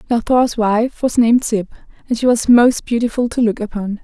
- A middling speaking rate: No, fast, 210 wpm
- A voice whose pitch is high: Yes, high, 230 Hz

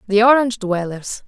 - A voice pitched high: Yes, high, 215 Hz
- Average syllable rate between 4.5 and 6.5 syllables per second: Yes, 5.4 syllables/s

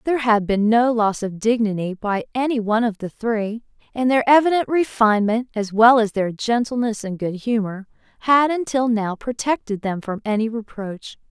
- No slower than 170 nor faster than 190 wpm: Yes, average, 175 wpm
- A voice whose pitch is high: Yes, high, 225 Hz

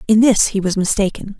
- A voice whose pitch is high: Yes, high, 200 Hz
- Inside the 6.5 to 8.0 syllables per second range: No, 5.7 syllables/s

